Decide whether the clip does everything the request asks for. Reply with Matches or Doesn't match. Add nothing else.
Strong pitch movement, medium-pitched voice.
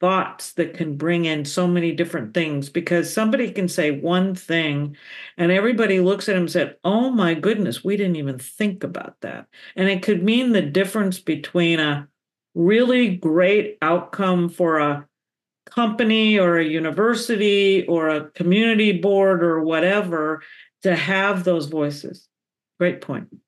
Doesn't match